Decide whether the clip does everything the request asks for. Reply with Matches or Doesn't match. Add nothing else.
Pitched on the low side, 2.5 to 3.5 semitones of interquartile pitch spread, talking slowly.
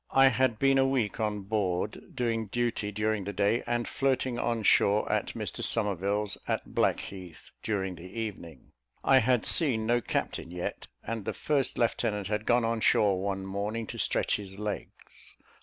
Doesn't match